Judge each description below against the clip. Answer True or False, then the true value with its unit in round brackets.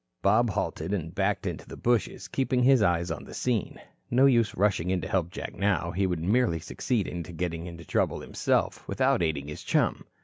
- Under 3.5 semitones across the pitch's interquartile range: False (5.0 semitones)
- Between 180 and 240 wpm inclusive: True (200 wpm)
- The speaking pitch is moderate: False (95 Hz)